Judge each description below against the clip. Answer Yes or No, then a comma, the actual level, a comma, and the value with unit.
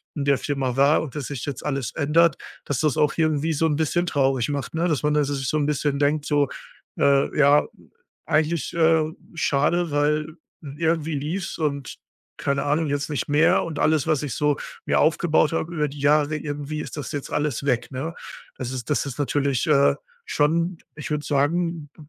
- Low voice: No, medium, 150 Hz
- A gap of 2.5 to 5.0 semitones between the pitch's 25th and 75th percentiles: No, narrow, 2.0 semitones